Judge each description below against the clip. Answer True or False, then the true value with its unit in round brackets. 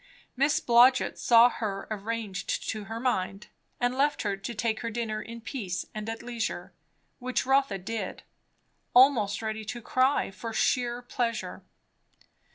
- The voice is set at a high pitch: True (230 Hz)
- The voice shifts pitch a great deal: False (2.5 semitones)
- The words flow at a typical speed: True (145 wpm)